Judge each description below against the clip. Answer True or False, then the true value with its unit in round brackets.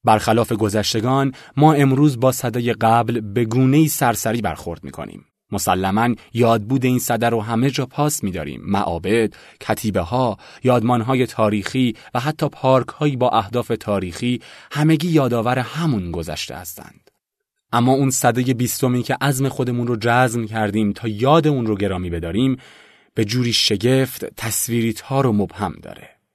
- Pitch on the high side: False (120 Hz)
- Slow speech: False (150 wpm)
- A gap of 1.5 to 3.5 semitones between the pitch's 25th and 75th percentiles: True (3.1 semitones)